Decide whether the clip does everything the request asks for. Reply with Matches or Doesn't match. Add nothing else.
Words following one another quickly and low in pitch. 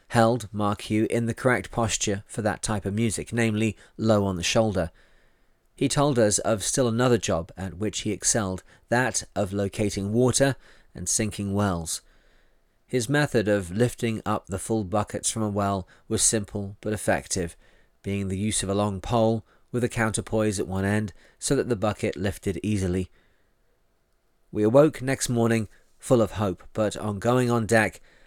Doesn't match